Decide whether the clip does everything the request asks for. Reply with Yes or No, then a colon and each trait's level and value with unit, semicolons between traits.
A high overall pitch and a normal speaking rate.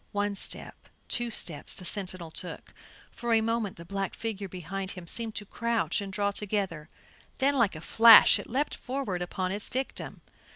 Yes: high, 200 Hz; average, 175 wpm